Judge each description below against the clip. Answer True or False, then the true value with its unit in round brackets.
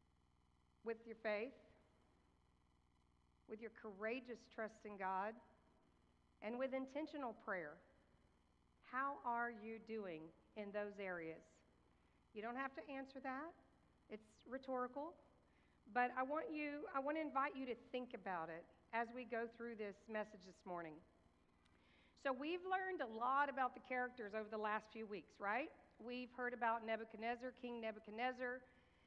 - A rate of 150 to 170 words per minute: False (140 wpm)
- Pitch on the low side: False (225 Hz)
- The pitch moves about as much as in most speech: False (7.5 semitones)